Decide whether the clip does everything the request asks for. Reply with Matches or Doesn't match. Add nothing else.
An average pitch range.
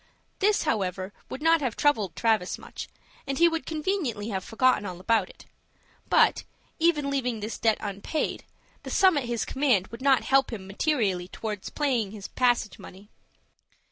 Doesn't match